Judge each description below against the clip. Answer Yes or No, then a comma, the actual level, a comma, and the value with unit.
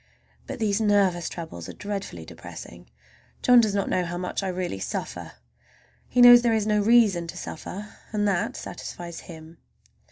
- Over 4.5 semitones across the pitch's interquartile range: No, average, 3.7 semitones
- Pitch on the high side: Yes, high, 200 Hz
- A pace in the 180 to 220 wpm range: No, average, 165 wpm